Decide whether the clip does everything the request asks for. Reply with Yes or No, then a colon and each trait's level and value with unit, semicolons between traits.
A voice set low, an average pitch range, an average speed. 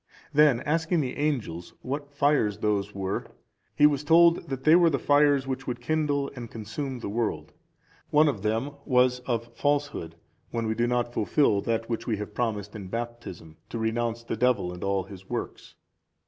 Yes: low, 120 Hz; average, 4.9 semitones; average, 175 wpm